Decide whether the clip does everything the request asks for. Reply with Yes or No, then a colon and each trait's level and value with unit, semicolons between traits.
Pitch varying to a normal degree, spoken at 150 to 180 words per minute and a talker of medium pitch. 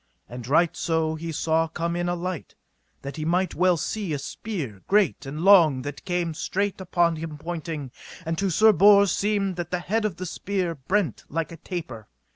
No: average, 3.2 semitones; average, 195 wpm; medium, 170 Hz